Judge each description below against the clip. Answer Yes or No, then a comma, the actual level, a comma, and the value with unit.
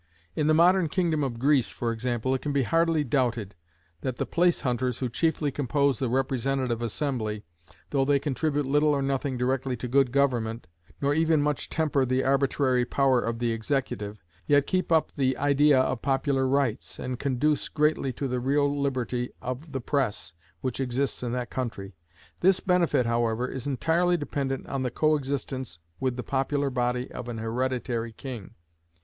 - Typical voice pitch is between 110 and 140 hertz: Yes, low, 135 Hz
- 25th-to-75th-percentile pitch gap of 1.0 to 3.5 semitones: Yes, average, 2.8 semitones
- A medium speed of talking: Yes, average, 170 wpm